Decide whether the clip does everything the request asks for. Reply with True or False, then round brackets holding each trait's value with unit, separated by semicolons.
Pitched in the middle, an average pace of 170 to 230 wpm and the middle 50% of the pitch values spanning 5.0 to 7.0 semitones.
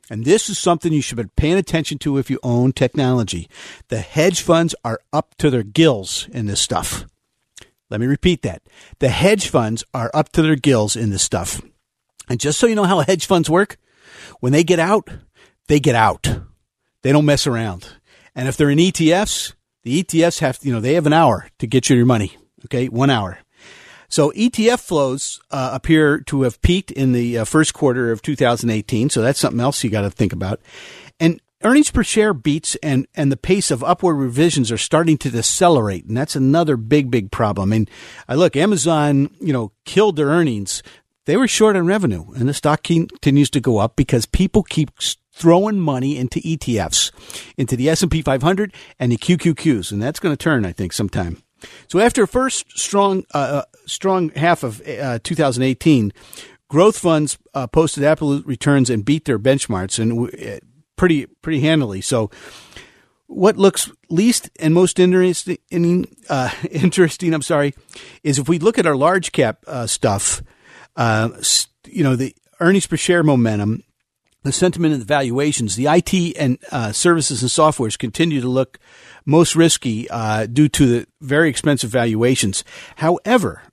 True (145 Hz; 185 wpm; 5.6 semitones)